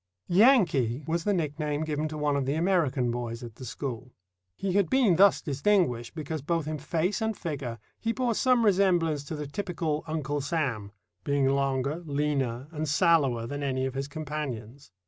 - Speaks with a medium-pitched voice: Yes, medium, 150 Hz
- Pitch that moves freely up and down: No, average, 4.1 semitones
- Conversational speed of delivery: Yes, average, 175 wpm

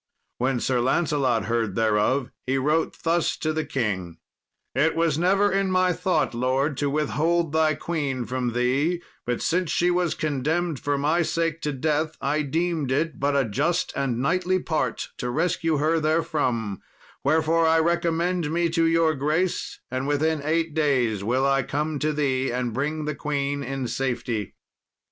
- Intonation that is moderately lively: Yes, average, 4.0 semitones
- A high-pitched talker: No, medium, 150 Hz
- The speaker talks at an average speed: Yes, average, 165 wpm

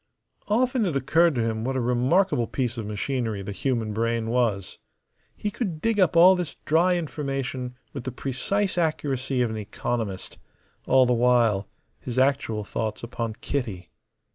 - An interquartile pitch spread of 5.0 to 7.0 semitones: Yes, wide, 5.5 semitones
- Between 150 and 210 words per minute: Yes, average, 160 wpm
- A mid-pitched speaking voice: No, low, 125 Hz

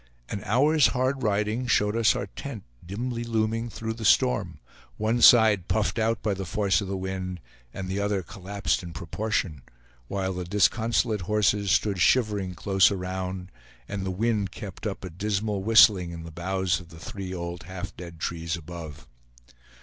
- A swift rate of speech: No, average, 165 wpm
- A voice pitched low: Yes, low, 100 Hz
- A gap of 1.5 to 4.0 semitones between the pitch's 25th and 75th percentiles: Yes, average, 3.2 semitones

